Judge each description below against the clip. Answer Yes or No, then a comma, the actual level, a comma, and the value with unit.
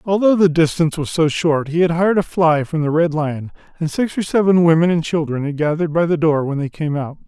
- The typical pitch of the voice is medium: Yes, medium, 160 Hz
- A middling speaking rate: No, fast, 255 wpm